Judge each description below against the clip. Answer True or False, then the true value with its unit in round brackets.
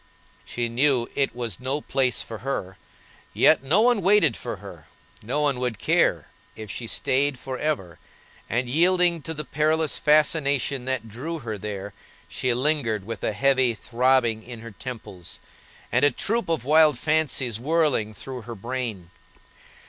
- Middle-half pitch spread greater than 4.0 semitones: True (4.6 semitones)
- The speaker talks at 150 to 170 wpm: True (155 wpm)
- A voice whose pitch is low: True (130 Hz)